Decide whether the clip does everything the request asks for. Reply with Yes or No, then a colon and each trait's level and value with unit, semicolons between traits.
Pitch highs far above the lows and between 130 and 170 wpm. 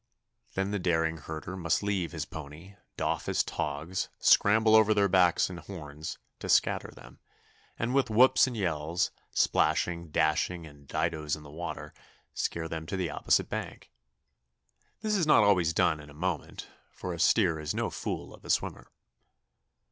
No: average, 4.4 semitones; average, 165 wpm